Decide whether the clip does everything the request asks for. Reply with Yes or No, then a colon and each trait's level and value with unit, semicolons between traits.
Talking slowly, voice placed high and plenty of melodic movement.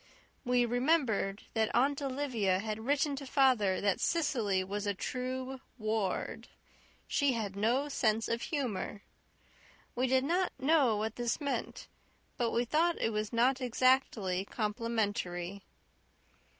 No: slow, 130 wpm; high, 235 Hz; average, 4.3 semitones